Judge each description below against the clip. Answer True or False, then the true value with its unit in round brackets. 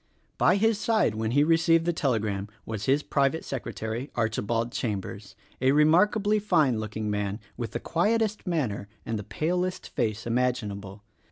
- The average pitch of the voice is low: True (125 Hz)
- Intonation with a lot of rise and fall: True (7.6 semitones)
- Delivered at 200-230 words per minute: False (155 wpm)